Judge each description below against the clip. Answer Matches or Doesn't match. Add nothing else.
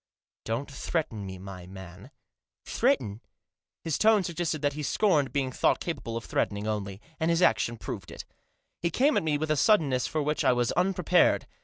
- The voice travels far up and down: Matches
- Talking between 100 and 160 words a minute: Doesn't match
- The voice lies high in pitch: Doesn't match